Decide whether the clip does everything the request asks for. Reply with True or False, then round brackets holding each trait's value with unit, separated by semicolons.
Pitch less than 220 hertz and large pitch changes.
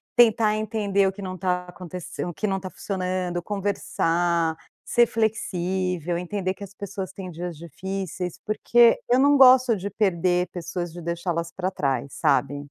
False (185 Hz; 2.7 semitones)